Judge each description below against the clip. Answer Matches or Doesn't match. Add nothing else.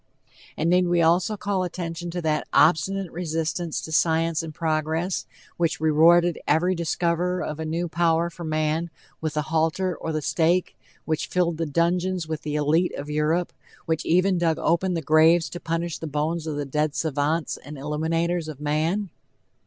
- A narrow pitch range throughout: Matches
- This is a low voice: Doesn't match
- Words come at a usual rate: Matches